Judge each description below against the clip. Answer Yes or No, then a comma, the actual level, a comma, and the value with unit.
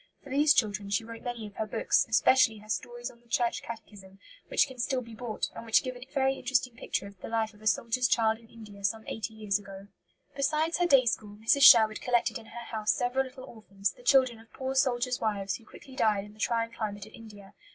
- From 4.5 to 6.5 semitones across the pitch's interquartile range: No, average, 3.0 semitones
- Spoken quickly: Yes, fast, 235 wpm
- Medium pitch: No, high, 230 Hz